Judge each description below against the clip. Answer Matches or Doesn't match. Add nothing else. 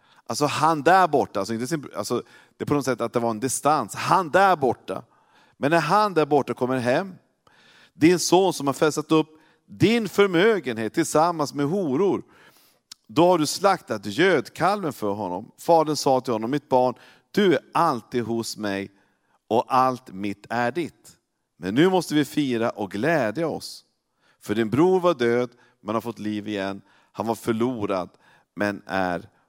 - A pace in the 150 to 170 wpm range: Matches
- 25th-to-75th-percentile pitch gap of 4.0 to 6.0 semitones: Matches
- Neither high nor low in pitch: Doesn't match